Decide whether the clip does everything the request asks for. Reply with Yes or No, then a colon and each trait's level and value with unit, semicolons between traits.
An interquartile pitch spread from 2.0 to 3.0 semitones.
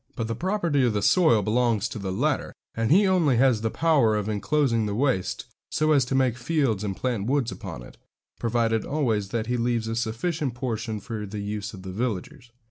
No: average, 4.2 semitones